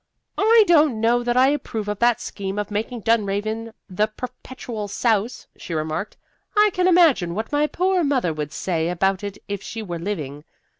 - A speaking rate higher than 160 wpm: Yes, average, 180 wpm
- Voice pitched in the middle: No, high, 220 Hz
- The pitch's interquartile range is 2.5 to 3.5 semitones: No, average, 4.9 semitones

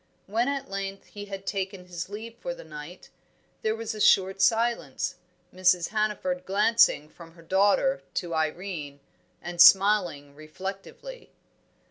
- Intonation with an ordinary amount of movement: Yes, average, 3.7 semitones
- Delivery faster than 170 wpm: No, slow, 135 wpm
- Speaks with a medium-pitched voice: No, high, 195 Hz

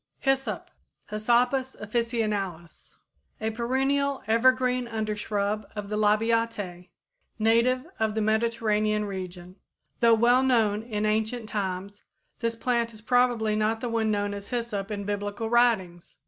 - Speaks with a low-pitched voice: No, high, 220 Hz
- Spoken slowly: Yes, slow, 130 wpm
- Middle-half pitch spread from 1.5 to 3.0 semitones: Yes, narrow, 2.4 semitones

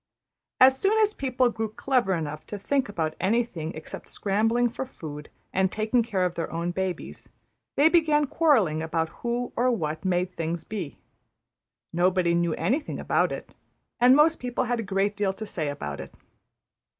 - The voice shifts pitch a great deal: Yes, wide, 6.5 semitones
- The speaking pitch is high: Yes, high, 205 Hz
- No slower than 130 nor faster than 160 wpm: No, average, 170 wpm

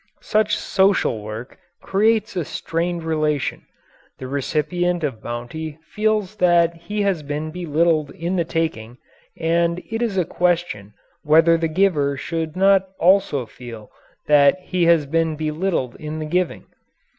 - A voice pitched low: No, medium, 165 Hz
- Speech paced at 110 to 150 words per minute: Yes, average, 140 wpm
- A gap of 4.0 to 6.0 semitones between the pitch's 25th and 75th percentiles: No, average, 3.4 semitones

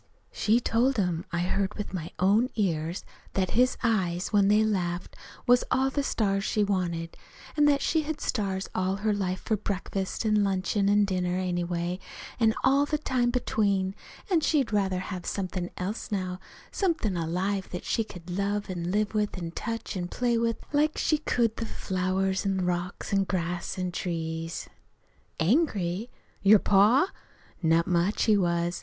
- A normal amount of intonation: Yes, average, 3.6 semitones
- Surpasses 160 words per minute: Yes, average, 170 wpm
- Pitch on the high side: Yes, high, 195 Hz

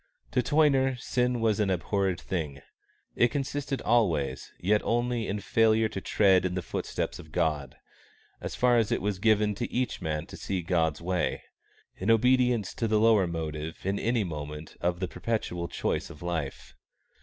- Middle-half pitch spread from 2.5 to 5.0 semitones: No, wide, 5.4 semitones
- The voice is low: Yes, low, 100 Hz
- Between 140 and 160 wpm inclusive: No, average, 175 wpm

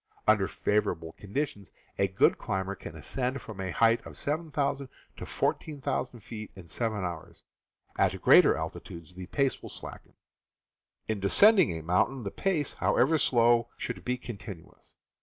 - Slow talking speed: No, average, 150 wpm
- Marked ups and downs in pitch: Yes, wide, 6.1 semitones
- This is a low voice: Yes, low, 110 Hz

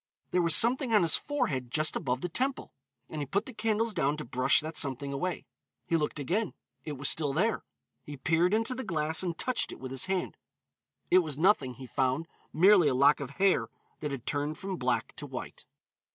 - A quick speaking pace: Yes, fast, 210 wpm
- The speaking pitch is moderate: Yes, medium, 160 Hz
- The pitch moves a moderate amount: No, wide, 5.8 semitones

